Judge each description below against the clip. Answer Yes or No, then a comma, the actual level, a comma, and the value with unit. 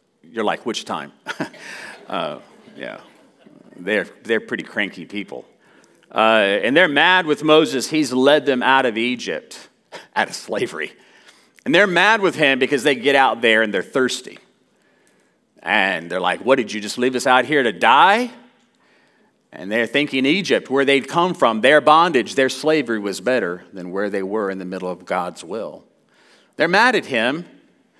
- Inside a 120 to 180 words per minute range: Yes, average, 170 wpm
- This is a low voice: Yes, low, 130 Hz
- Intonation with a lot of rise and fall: Yes, wide, 6.3 semitones